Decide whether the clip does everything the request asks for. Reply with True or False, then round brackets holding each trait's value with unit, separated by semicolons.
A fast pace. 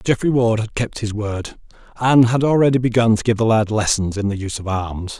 True (230 wpm)